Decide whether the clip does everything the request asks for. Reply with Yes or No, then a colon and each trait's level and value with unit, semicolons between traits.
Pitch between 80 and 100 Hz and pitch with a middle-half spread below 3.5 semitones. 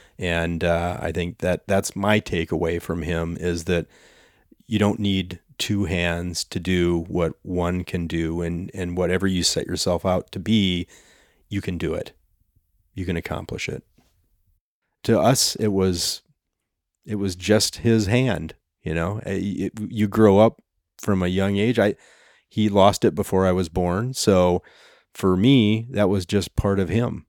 Yes: very low, 95 Hz; average, 2.9 semitones